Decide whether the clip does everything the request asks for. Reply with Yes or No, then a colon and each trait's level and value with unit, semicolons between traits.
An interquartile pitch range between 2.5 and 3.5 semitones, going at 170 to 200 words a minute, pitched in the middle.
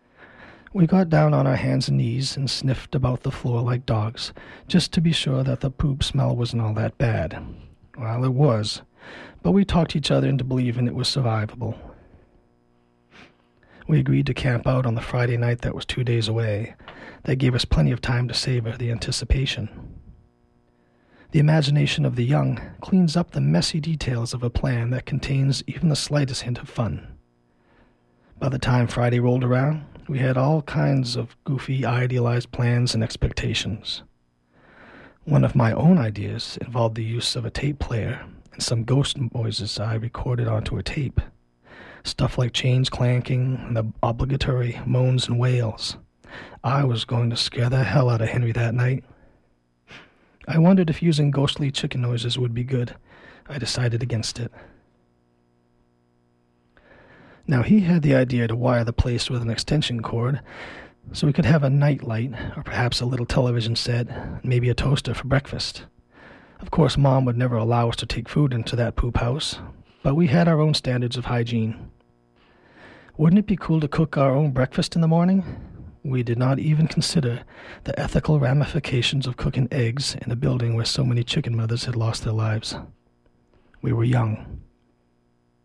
No: average, 3.2 semitones; average, 175 wpm; low, 125 Hz